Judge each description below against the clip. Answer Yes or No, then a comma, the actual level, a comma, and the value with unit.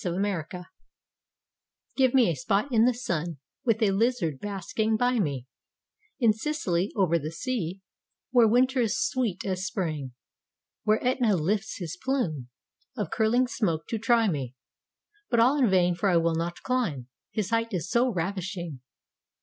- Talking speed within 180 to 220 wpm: No, average, 155 wpm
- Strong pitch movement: Yes, wide, 5.7 semitones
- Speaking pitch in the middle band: No, high, 200 Hz